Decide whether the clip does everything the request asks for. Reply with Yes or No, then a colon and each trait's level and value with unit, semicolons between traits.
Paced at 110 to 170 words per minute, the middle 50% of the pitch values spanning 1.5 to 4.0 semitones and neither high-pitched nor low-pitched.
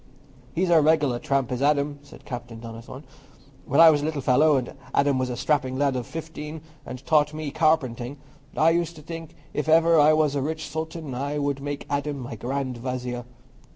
No: average, 195 wpm; average, 3.4 semitones; medium, 145 Hz